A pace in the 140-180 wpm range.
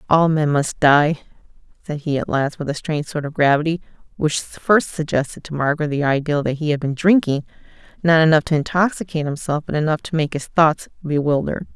No: average, 190 wpm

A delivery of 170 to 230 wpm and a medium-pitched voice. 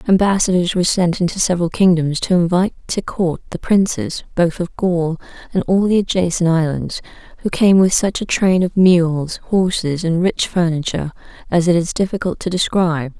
Yes: average, 175 wpm; medium, 175 Hz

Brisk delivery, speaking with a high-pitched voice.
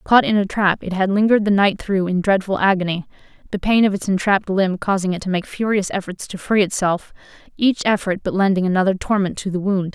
Yes: fast, 225 wpm; high, 195 Hz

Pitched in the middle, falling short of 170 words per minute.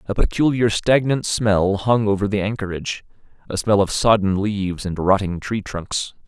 No: low, 100 Hz; average, 155 wpm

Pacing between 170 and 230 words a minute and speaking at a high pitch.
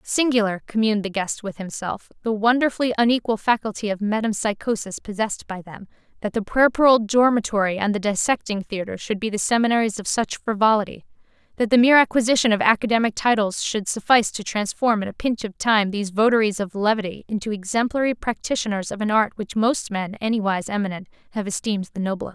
Yes: average, 175 wpm; high, 215 Hz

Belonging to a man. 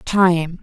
No: female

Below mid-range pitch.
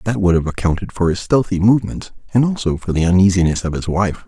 Yes: very low, 95 Hz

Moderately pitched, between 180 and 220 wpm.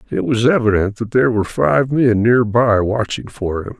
No: low, 115 Hz; fast, 205 wpm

